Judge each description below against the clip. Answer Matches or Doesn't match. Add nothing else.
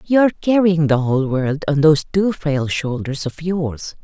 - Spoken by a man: Doesn't match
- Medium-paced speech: Matches